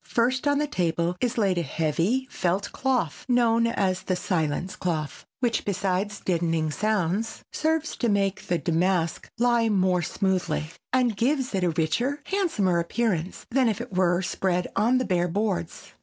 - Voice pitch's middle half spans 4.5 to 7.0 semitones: Yes, average, 5.3 semitones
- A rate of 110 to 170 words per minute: Yes, average, 160 wpm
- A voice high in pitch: Yes, high, 195 Hz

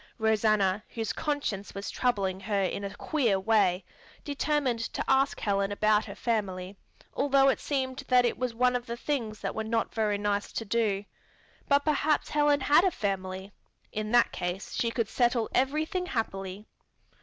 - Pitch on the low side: No, high, 225 Hz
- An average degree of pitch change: Yes, average, 4.8 semitones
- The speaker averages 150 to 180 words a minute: Yes, average, 165 wpm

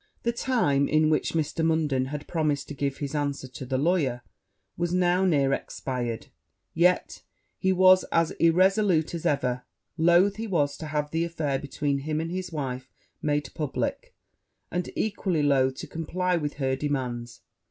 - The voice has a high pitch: No, medium, 150 Hz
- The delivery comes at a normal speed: Yes, average, 165 wpm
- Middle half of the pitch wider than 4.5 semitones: No, average, 4.0 semitones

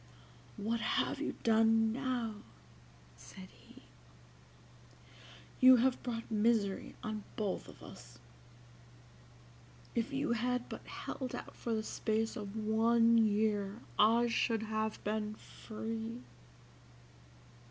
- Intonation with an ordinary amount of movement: No, narrow, 1.5 semitones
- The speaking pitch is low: No, high, 225 Hz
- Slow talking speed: Yes, slow, 110 wpm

